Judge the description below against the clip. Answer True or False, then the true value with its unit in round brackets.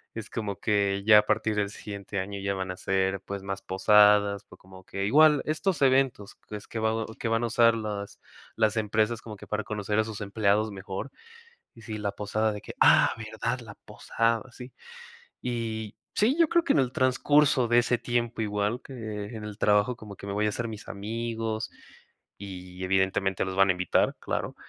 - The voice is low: True (105 Hz)